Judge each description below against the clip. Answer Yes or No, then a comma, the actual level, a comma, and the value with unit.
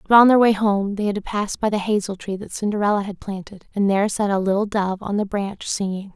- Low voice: No, high, 200 Hz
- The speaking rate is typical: No, fast, 265 wpm